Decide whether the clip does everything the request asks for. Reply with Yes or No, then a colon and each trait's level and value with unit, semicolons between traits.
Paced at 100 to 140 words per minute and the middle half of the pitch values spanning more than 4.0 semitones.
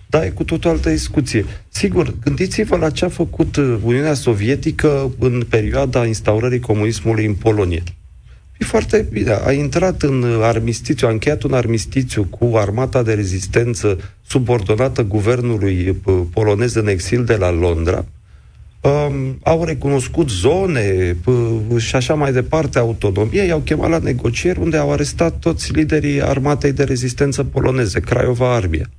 Yes: average, 135 wpm; average, 5.2 semitones